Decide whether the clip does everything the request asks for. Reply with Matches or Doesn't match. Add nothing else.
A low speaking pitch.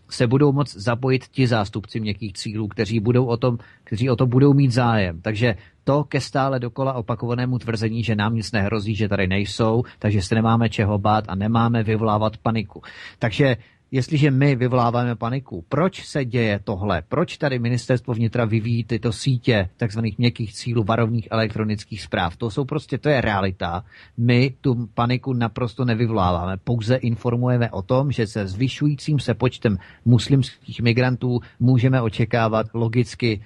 Matches